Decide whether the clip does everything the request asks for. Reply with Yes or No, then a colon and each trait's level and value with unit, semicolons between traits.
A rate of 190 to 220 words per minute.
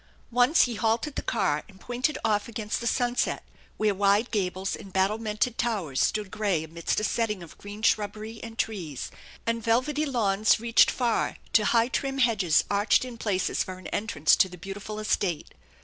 No: average, 175 wpm